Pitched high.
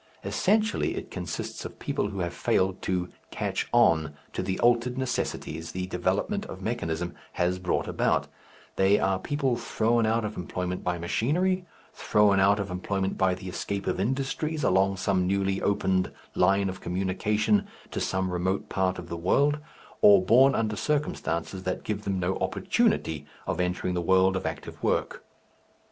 No: very low, 95 Hz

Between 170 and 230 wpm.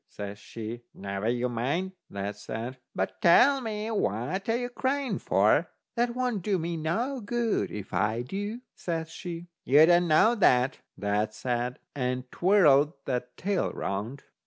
No: average, 155 wpm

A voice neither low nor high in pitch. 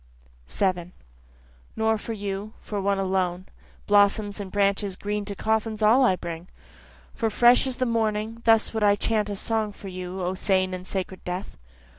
No: high, 205 Hz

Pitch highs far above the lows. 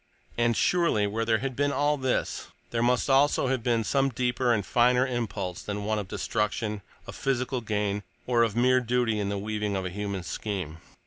No: average, 3.5 semitones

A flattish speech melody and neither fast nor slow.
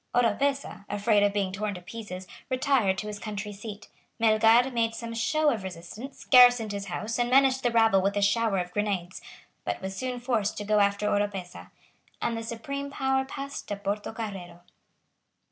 No: average, 3.3 semitones; average, 175 wpm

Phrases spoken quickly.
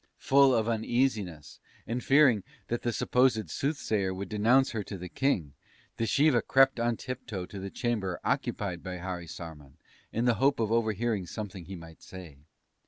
No: average, 160 wpm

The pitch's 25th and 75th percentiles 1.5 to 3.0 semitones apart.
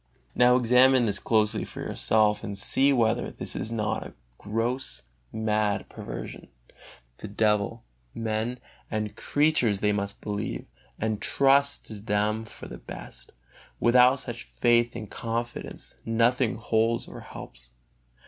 Yes: narrow, 2.5 semitones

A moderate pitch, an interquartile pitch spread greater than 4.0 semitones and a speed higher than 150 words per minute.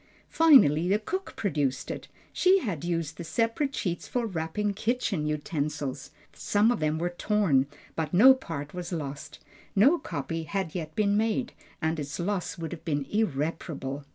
Yes: medium, 170 Hz; wide, 5.6 semitones; average, 160 wpm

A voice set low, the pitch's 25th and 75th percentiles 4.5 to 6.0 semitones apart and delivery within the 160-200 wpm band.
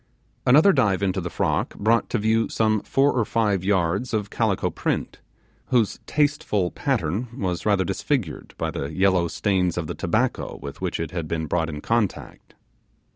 Yes: low, 100 Hz; average, 4.8 semitones; average, 170 wpm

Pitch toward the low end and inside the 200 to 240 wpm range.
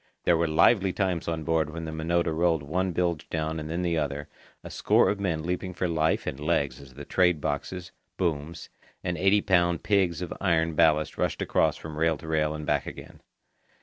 Yes: very low, 80 Hz; fast, 205 wpm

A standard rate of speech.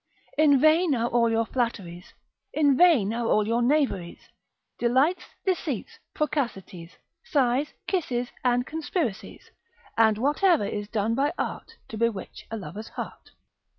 No: slow, 130 wpm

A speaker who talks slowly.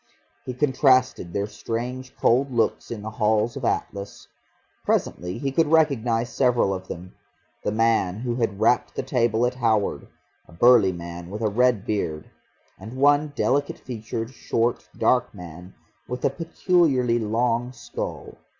No: average, 150 wpm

